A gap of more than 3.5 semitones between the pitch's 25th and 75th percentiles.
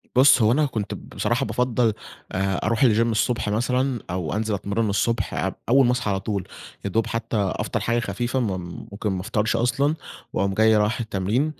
No: average, 3.1 semitones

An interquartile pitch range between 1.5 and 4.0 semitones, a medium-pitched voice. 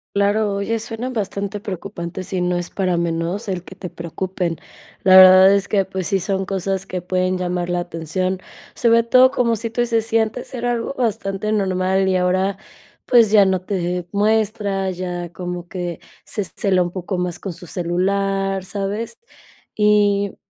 No: narrow, 2.5 semitones; high, 195 Hz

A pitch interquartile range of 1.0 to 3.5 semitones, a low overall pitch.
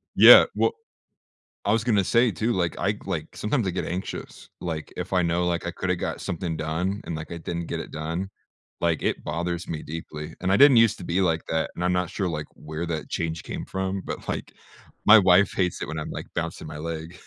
Yes: average, 2.9 semitones; very low, 85 Hz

